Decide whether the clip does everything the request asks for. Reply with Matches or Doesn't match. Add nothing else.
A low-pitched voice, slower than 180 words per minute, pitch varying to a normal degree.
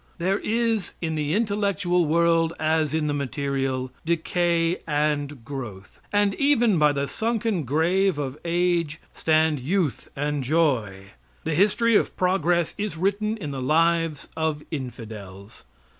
Doesn't match